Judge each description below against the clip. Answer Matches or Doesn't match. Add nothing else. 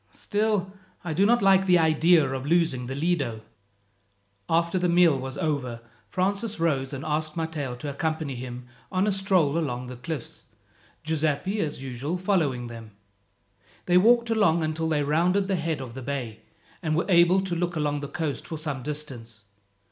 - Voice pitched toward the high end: Doesn't match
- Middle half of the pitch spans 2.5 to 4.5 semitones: Doesn't match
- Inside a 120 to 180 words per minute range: Matches